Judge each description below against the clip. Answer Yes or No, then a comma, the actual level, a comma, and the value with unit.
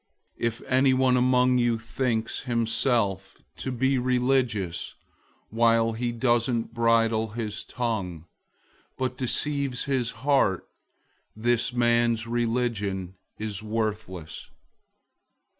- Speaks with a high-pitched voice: No, low, 115 Hz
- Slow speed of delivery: Yes, slow, 95 wpm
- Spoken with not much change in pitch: Yes, narrow, 2.3 semitones